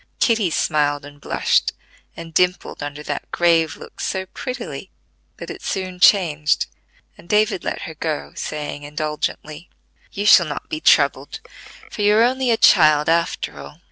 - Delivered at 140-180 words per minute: Yes, average, 155 wpm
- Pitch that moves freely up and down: No, average, 4.4 semitones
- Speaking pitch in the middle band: Yes, medium, 160 Hz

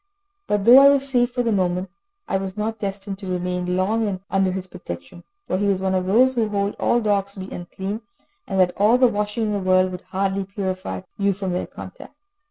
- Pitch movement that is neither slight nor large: No, narrow, 2.2 semitones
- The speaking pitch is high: Yes, high, 195 Hz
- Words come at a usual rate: No, fast, 220 wpm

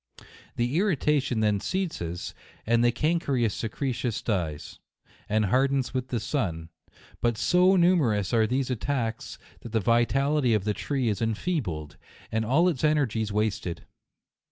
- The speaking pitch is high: No, low, 120 Hz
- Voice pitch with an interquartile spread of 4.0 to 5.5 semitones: Yes, average, 4.9 semitones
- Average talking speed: Yes, average, 150 wpm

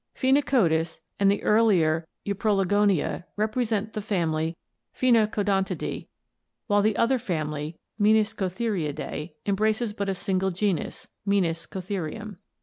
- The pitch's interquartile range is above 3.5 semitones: Yes, average, 3.9 semitones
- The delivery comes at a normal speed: No, slow, 105 wpm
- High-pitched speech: Yes, high, 200 Hz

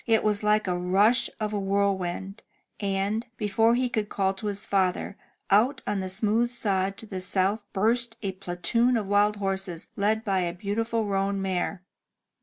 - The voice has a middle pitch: No, high, 200 Hz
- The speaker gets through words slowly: No, average, 180 wpm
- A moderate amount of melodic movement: No, narrow, 2.2 semitones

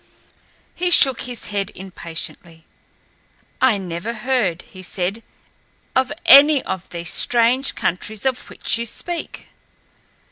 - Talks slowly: Yes, slow, 115 wpm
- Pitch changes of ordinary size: No, wide, 6.3 semitones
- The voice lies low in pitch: No, high, 220 Hz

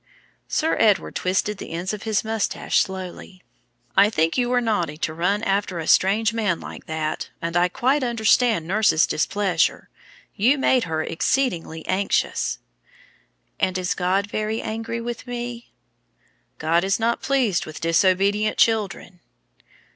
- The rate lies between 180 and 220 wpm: No, average, 140 wpm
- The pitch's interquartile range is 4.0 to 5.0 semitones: Yes, average, 4.3 semitones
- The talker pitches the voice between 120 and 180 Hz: No, high, 200 Hz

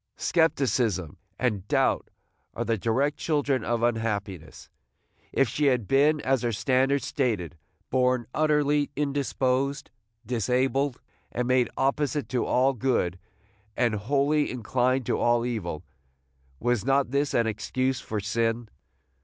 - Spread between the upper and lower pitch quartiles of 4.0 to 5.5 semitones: No, average, 3.3 semitones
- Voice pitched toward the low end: Yes, low, 125 Hz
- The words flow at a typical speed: No, slow, 125 wpm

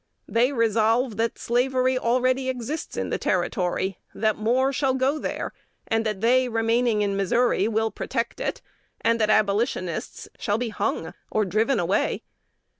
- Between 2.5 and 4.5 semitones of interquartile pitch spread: Yes, average, 3.0 semitones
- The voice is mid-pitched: No, high, 230 Hz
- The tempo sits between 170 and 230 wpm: No, average, 150 wpm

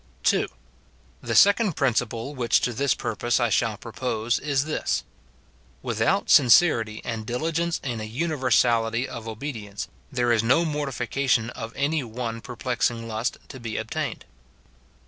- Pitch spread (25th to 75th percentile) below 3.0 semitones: No, average, 3.4 semitones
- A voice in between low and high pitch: No, low, 120 Hz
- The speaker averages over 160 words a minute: No, average, 140 wpm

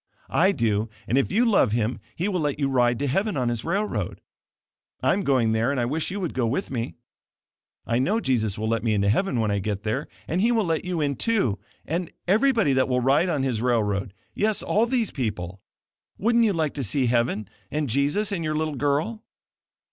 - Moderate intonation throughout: No, wide, 8.1 semitones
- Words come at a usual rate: No, fast, 215 wpm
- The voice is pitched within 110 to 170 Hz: Yes, medium, 140 Hz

